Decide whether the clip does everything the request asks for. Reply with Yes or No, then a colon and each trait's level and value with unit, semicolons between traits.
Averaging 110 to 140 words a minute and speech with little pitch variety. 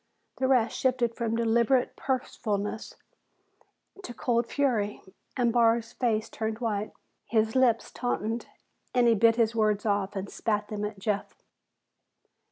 Yes: slow, 135 wpm; narrow, 2.1 semitones